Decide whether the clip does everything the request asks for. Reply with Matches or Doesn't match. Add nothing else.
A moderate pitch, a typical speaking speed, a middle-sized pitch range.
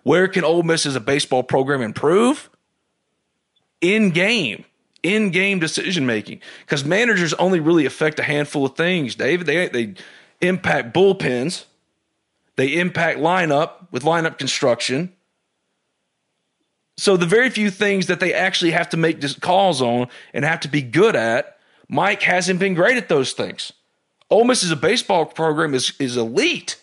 Matches